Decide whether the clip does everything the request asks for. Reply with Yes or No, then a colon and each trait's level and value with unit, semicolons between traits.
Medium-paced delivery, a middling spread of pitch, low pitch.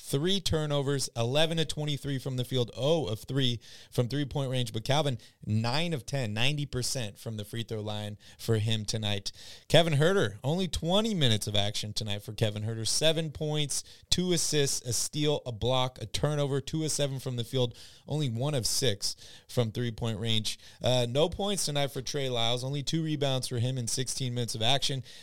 Yes: average, 190 wpm; average, 4.3 semitones; low, 125 Hz